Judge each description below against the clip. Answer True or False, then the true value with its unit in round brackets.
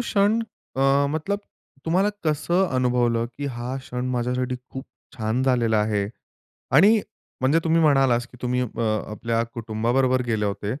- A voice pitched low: True (125 Hz)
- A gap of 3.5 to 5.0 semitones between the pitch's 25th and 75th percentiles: True (4.4 semitones)